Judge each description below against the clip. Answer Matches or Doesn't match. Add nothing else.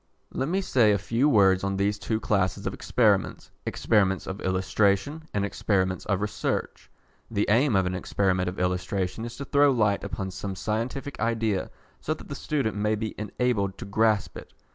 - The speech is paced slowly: Doesn't match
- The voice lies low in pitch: Matches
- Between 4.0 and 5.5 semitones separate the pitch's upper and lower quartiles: Doesn't match